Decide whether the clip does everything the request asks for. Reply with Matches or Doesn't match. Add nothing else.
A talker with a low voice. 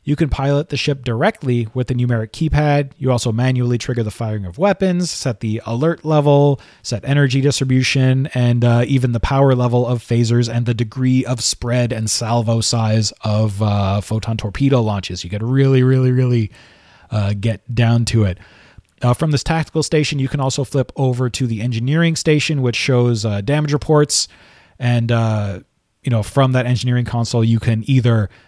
Matches